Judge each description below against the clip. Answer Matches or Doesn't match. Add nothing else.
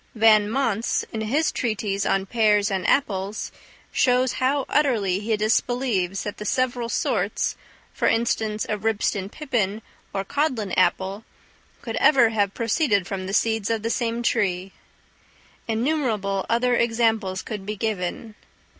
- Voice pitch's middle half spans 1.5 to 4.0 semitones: Matches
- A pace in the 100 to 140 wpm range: Matches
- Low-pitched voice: Doesn't match